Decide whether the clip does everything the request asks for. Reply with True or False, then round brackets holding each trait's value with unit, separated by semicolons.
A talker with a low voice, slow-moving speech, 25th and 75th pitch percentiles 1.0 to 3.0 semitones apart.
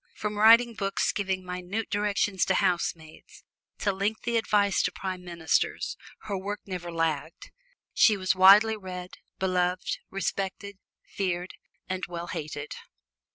False (190 Hz; 125 wpm; 2.4 semitones)